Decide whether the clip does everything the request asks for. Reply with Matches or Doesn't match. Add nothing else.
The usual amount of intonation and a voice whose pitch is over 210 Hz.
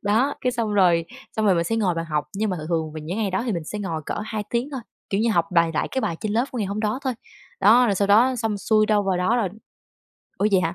Doesn't match